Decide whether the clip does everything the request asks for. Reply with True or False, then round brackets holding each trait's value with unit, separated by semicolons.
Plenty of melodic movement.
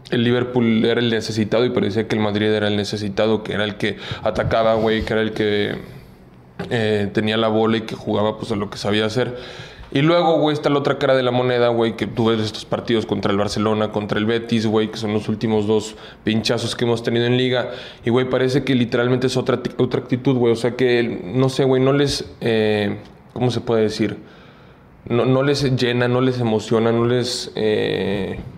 False (2.5 semitones)